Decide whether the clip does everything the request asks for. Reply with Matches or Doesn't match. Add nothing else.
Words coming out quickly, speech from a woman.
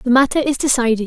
Matches